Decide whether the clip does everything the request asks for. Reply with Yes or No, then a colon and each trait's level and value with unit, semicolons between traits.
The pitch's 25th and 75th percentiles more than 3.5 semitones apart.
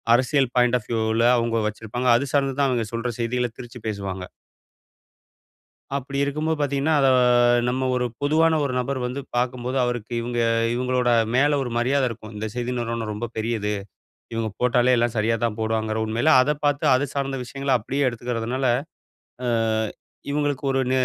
No: average, 3.0 semitones